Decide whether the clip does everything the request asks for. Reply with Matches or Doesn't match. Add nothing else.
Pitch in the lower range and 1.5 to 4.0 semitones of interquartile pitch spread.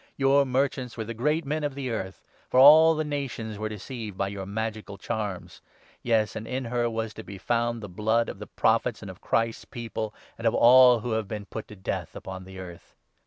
Matches